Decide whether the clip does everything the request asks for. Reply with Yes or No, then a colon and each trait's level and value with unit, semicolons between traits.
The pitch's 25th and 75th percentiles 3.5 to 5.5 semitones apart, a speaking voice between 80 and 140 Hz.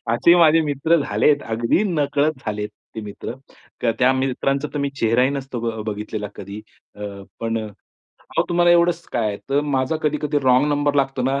Yes: average, 4.6 semitones; low, 135 Hz